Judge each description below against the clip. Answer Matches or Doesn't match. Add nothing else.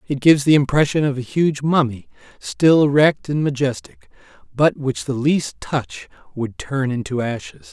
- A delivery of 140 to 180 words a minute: Matches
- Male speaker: Matches